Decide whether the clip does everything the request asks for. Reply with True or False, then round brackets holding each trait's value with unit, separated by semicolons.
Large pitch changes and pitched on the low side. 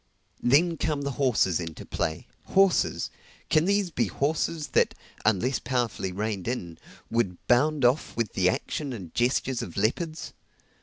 True (7.3 semitones; 125 Hz)